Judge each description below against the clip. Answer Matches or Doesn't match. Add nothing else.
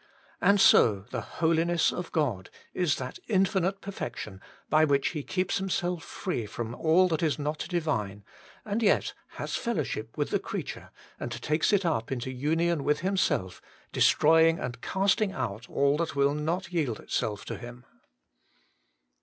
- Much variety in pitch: Matches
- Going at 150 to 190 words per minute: Matches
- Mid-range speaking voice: Matches